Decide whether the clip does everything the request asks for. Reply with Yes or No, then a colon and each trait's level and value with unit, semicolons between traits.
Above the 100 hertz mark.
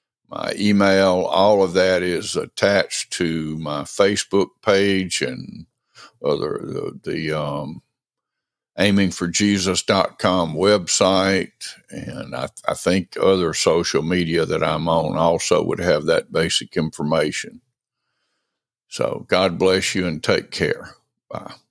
No: very low, 90 Hz